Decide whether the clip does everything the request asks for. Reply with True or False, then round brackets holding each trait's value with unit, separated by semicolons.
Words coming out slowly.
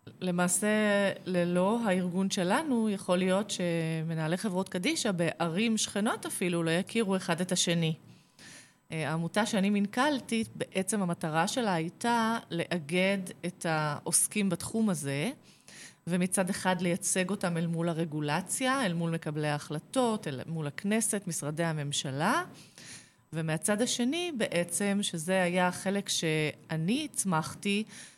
False (115 wpm)